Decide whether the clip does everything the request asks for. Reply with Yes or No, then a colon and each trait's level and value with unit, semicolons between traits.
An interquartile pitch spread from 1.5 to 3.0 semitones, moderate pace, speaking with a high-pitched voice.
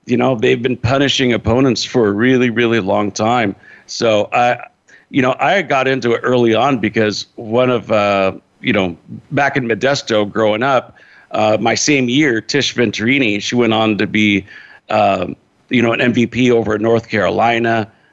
No: average, 2.7 semitones; average, 175 wpm; low, 115 Hz